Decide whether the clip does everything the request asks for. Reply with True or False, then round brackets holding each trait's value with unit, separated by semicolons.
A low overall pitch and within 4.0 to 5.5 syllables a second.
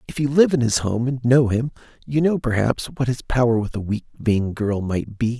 True (120 Hz; 5.0 syllables/s)